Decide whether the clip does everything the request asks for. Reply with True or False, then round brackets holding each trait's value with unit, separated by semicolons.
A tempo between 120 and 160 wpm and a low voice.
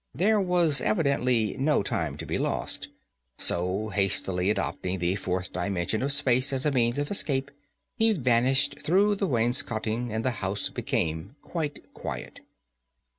True (145 wpm; 120 Hz)